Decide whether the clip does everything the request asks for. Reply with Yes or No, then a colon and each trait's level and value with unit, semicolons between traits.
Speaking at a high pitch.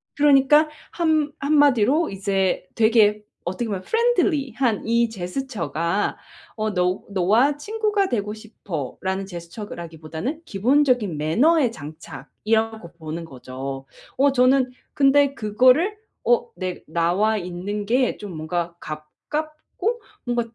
Yes: high, 220 Hz